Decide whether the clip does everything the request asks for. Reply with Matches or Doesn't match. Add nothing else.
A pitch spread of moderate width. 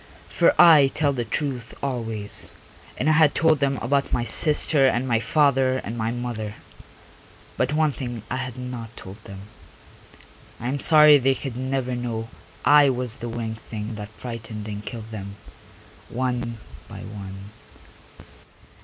Matches